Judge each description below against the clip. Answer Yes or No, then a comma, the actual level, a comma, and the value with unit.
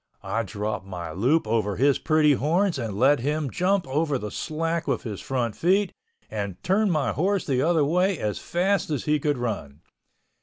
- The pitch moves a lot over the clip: Yes, wide, 7.1 semitones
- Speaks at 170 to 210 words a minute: Yes, average, 185 wpm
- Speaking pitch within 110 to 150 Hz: Yes, medium, 140 Hz